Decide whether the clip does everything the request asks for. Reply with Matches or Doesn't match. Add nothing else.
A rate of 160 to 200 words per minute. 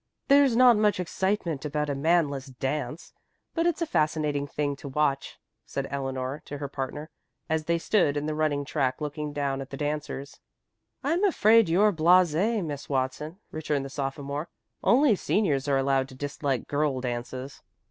Matches